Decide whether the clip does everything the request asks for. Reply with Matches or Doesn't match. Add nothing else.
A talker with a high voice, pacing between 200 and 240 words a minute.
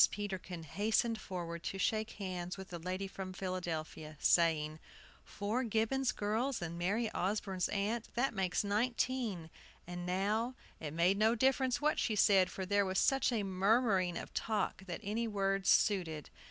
Doesn't match